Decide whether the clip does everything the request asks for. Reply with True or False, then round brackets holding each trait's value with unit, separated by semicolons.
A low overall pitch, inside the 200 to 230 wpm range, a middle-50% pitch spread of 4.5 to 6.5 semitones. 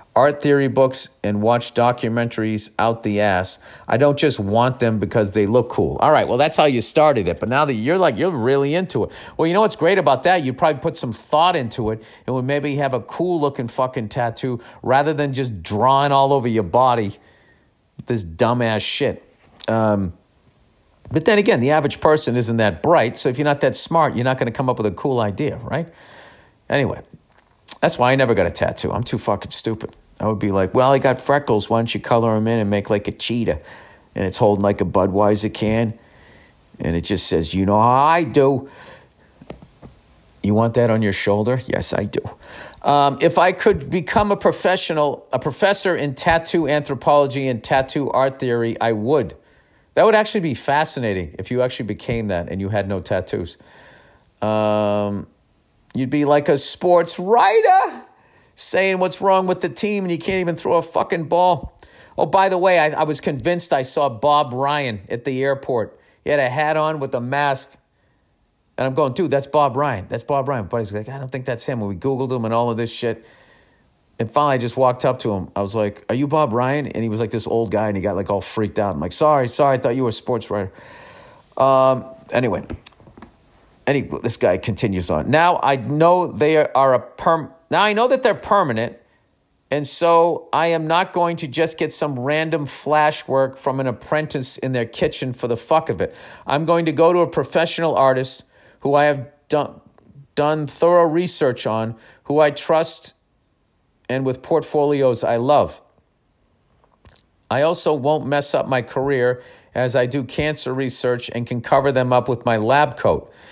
True (130 Hz; 205 wpm; 5.0 semitones)